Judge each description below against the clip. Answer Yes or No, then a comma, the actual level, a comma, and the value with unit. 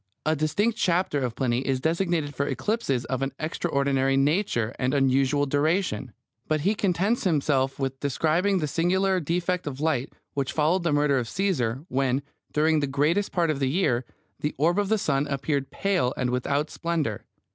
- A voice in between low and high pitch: Yes, medium, 145 Hz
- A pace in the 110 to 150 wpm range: No, average, 175 wpm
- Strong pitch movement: No, average, 4.3 semitones